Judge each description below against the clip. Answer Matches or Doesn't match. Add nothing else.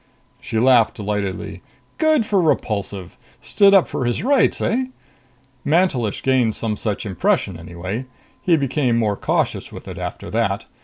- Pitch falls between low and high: Doesn't match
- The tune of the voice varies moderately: Doesn't match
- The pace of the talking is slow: Doesn't match